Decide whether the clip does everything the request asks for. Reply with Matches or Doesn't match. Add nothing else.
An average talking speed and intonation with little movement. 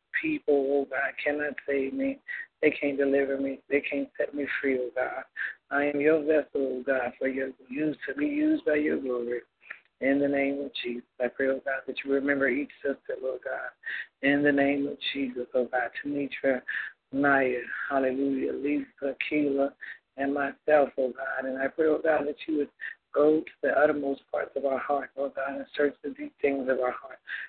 Matches